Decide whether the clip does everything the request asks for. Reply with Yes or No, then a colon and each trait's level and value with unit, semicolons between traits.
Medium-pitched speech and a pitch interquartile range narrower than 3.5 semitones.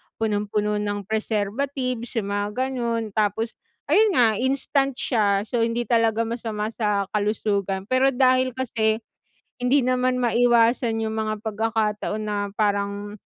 No: high, 225 Hz; average, 2.9 semitones